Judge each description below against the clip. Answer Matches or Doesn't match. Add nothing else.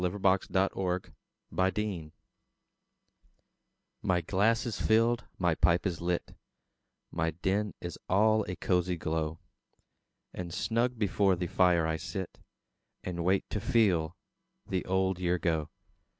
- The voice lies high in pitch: Doesn't match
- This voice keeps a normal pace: Doesn't match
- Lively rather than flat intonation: Doesn't match